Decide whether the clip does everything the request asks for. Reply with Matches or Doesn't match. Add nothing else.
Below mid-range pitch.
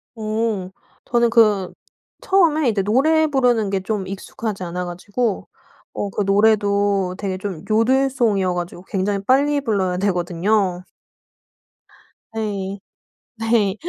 Doesn't match